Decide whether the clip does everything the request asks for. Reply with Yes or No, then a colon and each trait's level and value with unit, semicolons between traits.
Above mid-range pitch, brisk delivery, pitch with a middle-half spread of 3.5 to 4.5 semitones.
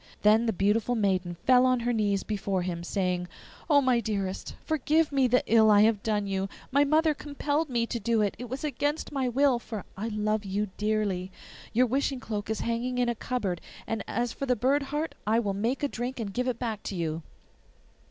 Yes: high, 230 Hz; fast, 210 wpm; average, 3.9 semitones